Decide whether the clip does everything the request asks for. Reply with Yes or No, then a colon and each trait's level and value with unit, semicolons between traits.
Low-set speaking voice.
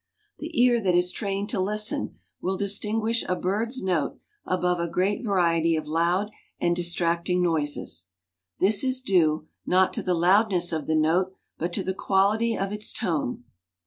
No: medium, 185 Hz